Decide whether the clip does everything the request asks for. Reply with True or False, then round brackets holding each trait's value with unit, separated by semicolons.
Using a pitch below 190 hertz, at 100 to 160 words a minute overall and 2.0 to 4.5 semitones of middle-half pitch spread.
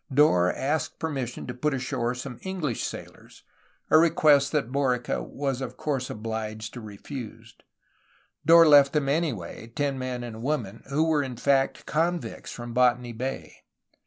True (135 Hz; 155 wpm; 3.5 semitones)